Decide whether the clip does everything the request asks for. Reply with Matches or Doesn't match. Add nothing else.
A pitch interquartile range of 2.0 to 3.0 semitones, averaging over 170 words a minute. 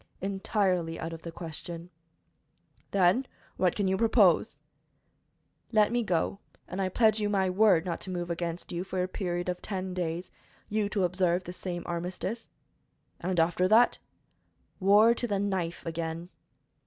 Doesn't match